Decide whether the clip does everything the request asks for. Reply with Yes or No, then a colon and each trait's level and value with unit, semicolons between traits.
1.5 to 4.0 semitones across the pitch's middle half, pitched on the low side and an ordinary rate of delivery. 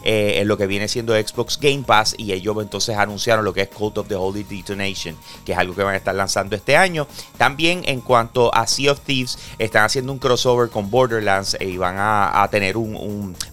No: average, 3.4 semitones; low, 105 Hz; fast, 230 wpm